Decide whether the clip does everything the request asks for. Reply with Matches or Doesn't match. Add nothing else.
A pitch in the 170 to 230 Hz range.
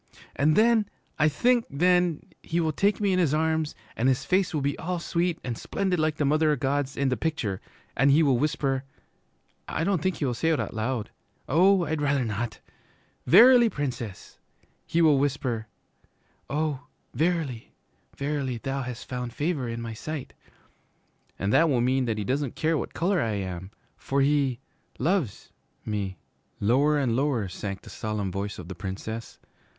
Doesn't match